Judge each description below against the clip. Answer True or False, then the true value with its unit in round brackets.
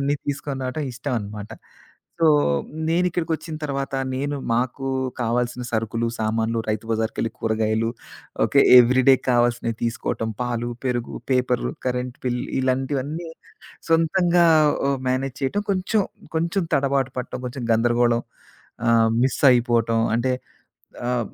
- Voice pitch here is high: False (125 Hz)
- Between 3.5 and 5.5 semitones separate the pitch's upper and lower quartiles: False (3.1 semitones)